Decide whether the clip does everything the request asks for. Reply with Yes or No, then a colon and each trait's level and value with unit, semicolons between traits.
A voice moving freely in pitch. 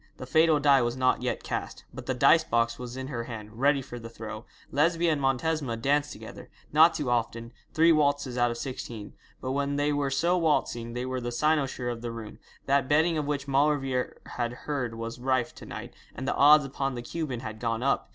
No: average, 3.5 semitones